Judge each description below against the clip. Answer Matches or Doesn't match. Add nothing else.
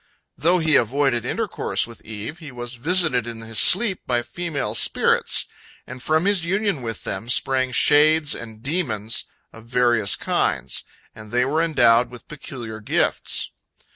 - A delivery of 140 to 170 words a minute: Matches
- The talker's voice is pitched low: Matches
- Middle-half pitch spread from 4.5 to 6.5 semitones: Matches